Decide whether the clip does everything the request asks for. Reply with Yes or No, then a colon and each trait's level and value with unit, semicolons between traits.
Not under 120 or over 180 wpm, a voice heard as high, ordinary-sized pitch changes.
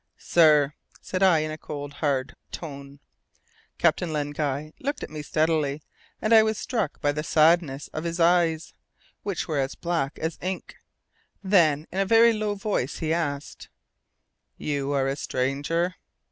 No: average, 160 wpm; medium, 155 Hz; average, 3.7 semitones